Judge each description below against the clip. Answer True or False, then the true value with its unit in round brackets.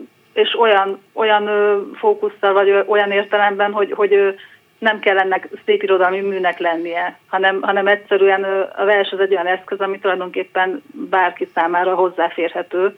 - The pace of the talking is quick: False (135 wpm)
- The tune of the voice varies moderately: False (1.9 semitones)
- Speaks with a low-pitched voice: False (195 Hz)